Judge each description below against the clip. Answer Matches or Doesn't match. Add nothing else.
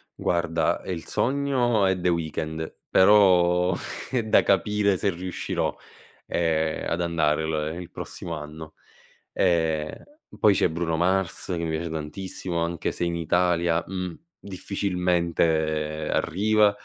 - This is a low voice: Matches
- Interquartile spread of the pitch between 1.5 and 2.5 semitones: Doesn't match